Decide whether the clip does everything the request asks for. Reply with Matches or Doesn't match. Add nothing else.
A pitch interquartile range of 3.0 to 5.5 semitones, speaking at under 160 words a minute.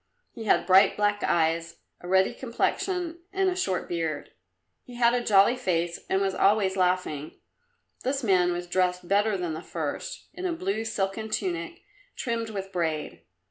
Doesn't match